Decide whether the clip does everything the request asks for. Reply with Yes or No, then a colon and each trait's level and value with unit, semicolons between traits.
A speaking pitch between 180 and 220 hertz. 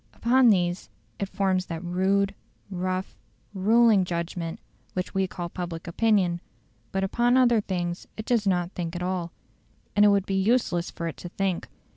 Yes: medium, 185 Hz